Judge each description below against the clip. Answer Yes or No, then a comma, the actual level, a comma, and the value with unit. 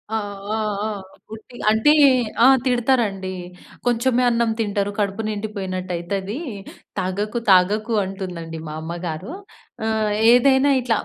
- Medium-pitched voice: No, high, 210 Hz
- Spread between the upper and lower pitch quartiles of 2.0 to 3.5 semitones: No, average, 4.1 semitones